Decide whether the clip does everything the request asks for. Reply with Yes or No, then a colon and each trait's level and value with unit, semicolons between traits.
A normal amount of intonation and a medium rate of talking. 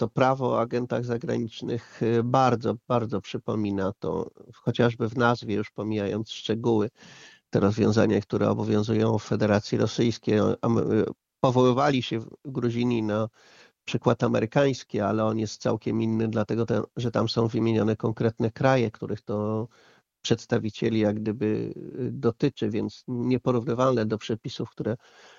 No: narrow, 2.1 semitones; average, 125 wpm